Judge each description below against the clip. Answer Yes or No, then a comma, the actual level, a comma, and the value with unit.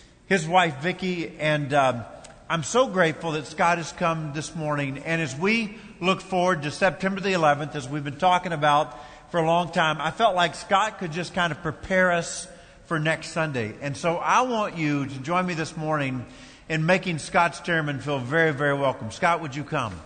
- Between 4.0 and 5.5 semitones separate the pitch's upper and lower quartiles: No, average, 3.4 semitones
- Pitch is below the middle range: No, medium, 165 Hz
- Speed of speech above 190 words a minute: Yes, average, 200 wpm